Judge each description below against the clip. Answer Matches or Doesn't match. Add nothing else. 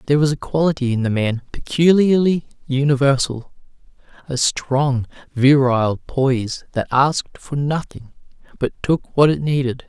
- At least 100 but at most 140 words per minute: Matches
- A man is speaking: Matches